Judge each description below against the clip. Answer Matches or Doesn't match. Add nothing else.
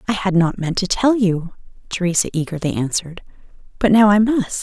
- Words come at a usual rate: Matches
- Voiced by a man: Doesn't match